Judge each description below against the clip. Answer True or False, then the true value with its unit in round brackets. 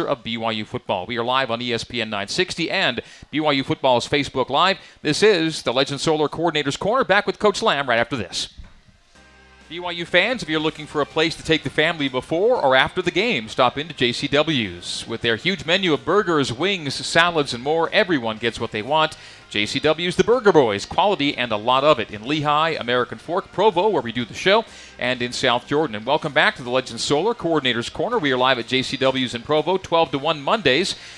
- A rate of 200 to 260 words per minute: True (205 wpm)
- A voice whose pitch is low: False (145 Hz)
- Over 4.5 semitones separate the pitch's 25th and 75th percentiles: True (5.0 semitones)